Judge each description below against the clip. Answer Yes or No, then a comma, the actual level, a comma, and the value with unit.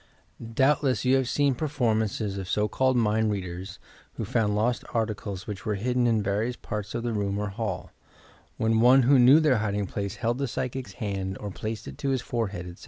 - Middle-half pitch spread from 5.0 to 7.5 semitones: No, average, 3.6 semitones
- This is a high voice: No, low, 110 Hz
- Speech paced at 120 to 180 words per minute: No, average, 200 wpm